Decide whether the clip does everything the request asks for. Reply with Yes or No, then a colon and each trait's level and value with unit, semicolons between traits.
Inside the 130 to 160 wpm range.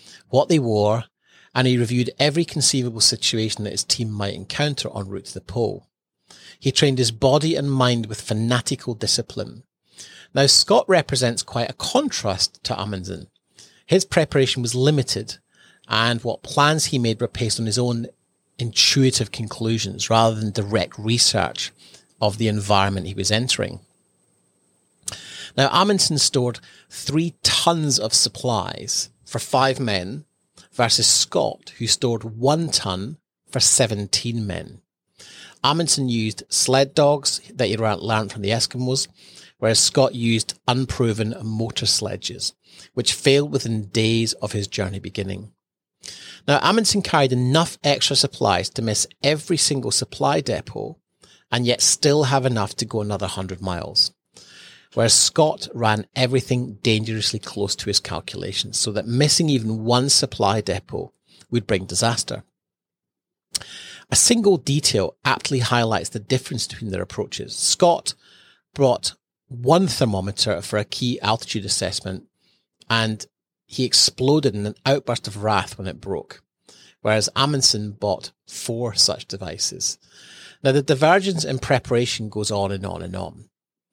Yes: average, 140 wpm